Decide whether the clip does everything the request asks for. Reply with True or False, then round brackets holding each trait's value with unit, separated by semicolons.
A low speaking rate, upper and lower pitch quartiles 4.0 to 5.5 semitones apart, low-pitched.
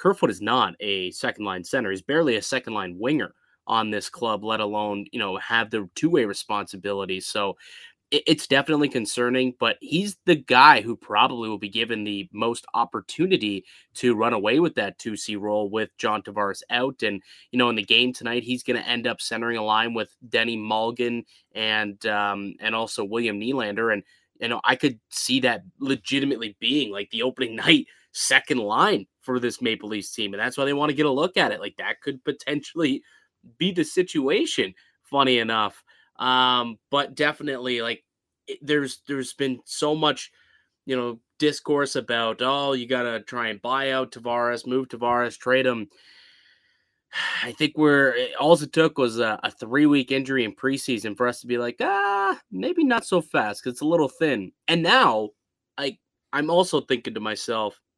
False (185 wpm; 4.7 semitones; 125 Hz)